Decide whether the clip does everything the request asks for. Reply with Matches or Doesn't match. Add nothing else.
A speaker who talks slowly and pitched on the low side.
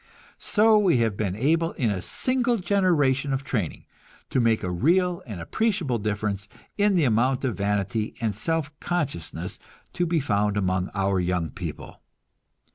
Doesn't match